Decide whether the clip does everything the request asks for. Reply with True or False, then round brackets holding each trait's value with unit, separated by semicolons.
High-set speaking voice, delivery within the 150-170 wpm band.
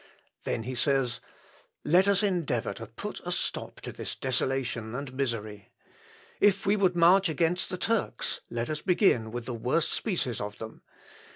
False (140 Hz; 165 wpm)